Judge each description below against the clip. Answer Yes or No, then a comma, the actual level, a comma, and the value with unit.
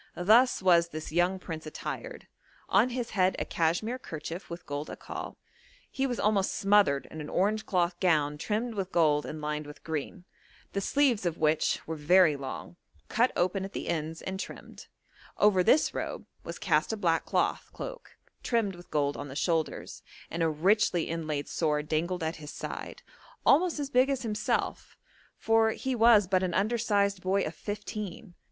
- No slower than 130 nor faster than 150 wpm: No, average, 175 wpm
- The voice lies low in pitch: No, medium, 185 Hz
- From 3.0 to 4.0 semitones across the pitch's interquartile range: No, average, 5.2 semitones